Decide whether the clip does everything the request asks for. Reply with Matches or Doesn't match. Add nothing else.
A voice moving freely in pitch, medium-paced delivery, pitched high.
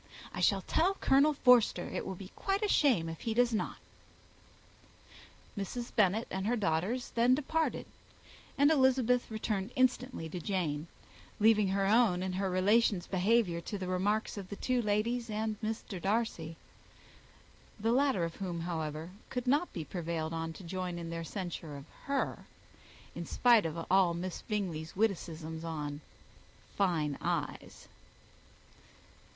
Matches